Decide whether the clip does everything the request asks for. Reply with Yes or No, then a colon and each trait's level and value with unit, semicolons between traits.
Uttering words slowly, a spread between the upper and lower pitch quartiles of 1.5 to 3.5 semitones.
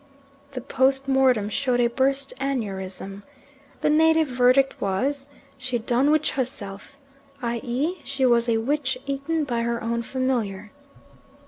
Yes: slow, 130 wpm; average, 2.8 semitones